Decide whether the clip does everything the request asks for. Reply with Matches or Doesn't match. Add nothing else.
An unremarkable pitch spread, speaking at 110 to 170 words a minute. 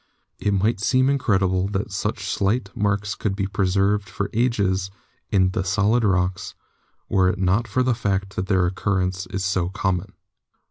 Doesn't match